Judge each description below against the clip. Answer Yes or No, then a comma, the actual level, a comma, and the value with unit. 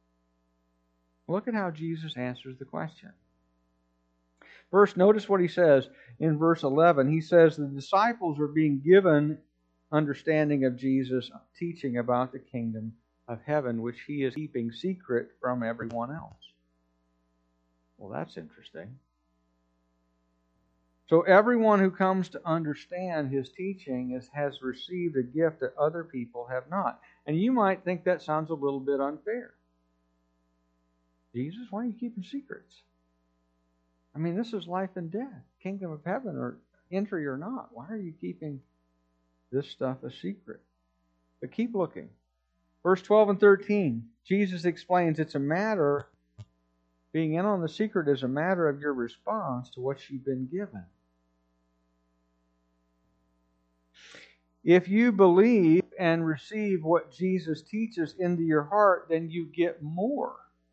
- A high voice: No, medium, 140 Hz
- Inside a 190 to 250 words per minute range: No, average, 140 wpm